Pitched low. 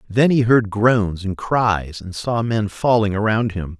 Yes: low, 105 Hz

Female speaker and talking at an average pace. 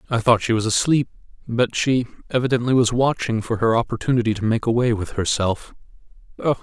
No: male; average, 165 wpm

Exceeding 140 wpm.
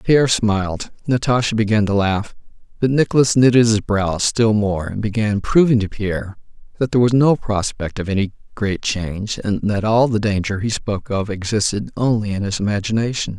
Yes: average, 180 wpm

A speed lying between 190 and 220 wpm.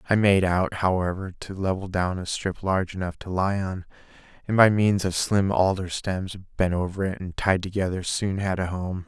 Yes: fast, 205 wpm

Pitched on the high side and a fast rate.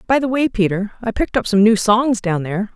Yes: high, 215 Hz; fast, 260 wpm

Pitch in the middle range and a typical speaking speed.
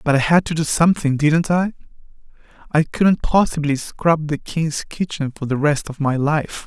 Yes: medium, 155 Hz; average, 180 wpm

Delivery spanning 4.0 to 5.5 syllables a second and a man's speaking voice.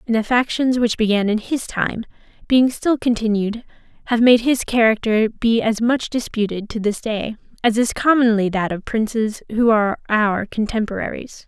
No: 4.8 syllables/s; female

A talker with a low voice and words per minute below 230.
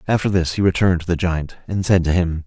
No: very low, 85 Hz; fast, 270 wpm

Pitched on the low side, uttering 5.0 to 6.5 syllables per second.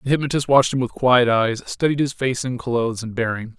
Yes: low, 125 Hz; 5.8 syllables/s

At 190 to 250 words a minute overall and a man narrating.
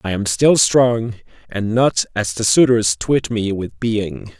No: average, 180 wpm; male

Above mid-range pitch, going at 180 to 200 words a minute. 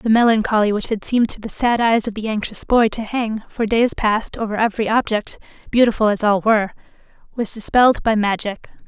Yes: high, 220 Hz; average, 195 wpm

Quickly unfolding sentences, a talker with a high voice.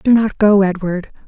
No: average, 190 wpm; high, 200 Hz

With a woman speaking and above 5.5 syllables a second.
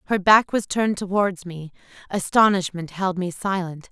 No: female; 4.8 syllables/s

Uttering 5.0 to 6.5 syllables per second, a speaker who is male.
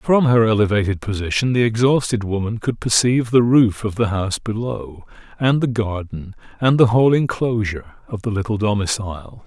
Yes: 5.4 syllables/s; male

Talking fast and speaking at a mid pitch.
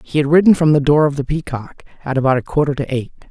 Yes: fast, 270 wpm; medium, 145 Hz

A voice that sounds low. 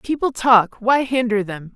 No: high, 230 Hz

